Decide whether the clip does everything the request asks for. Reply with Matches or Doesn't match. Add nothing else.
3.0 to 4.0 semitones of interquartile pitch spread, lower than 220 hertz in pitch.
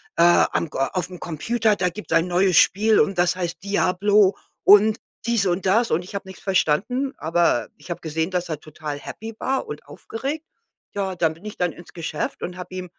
Matches